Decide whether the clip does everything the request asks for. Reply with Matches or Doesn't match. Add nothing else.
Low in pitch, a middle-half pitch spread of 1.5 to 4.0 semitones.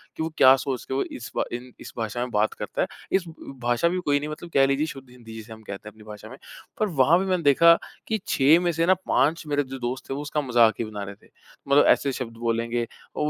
Doesn't match